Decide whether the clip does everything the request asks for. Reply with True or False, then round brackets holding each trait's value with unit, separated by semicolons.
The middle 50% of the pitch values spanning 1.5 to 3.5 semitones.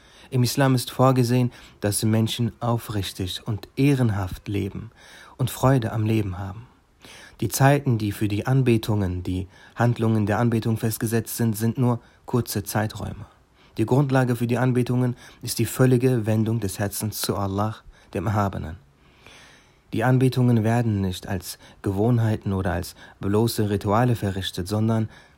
True (3.2 semitones)